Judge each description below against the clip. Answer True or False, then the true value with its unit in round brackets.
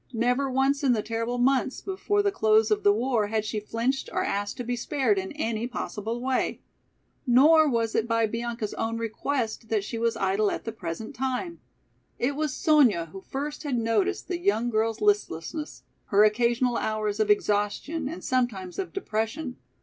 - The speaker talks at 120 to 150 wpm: False (180 wpm)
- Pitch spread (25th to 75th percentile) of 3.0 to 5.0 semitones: True (3.9 semitones)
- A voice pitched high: True (235 Hz)